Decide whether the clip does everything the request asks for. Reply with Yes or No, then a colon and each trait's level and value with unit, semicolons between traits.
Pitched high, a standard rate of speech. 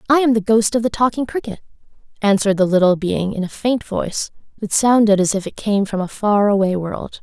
No: high, 210 Hz; fast, 225 wpm